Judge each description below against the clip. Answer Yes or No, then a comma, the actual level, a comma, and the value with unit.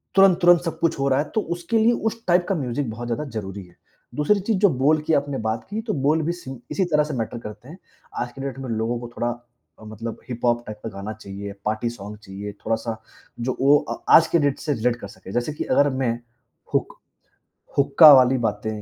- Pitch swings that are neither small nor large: No, wide, 6.0 semitones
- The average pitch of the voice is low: Yes, low, 130 Hz